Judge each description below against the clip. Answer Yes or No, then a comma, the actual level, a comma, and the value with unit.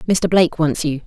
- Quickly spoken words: Yes, fast, 225 wpm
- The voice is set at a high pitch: No, medium, 160 Hz